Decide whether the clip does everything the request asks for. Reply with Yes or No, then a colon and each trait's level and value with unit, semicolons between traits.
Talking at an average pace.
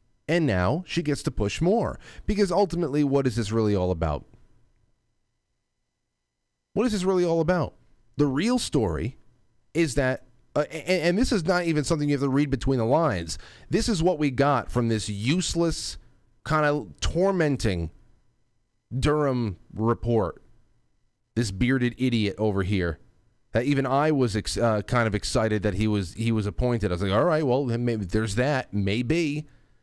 Yes: average, 170 wpm